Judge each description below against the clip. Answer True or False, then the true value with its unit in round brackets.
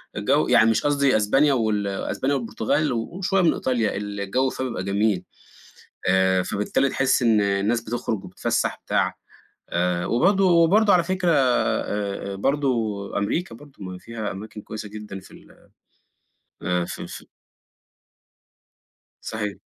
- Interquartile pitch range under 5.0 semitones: False (5.4 semitones)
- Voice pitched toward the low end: True (110 Hz)